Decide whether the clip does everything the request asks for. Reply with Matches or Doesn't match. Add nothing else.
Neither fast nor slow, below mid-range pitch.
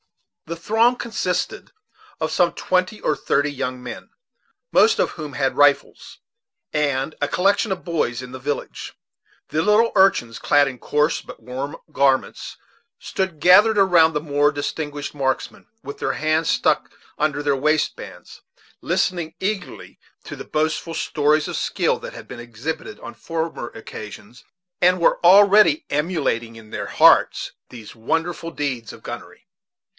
Doesn't match